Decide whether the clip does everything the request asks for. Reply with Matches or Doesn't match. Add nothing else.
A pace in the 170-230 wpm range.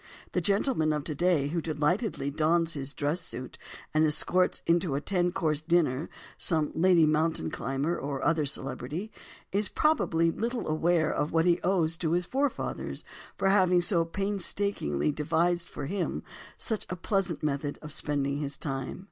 Doesn't match